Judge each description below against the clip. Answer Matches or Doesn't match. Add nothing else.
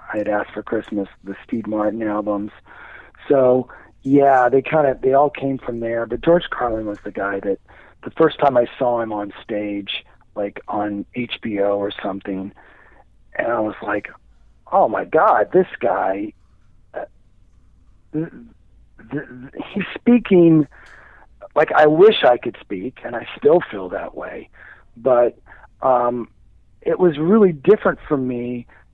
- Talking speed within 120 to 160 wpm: Matches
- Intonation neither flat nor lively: Doesn't match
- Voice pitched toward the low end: Matches